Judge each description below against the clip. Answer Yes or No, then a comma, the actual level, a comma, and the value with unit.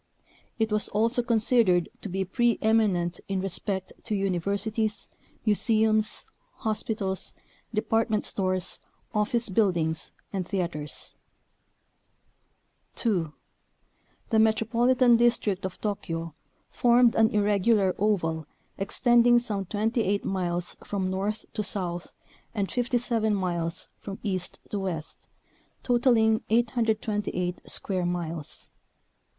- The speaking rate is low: Yes, slow, 100 wpm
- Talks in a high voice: Yes, high, 205 Hz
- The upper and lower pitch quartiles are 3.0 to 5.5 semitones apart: Yes, average, 3.3 semitones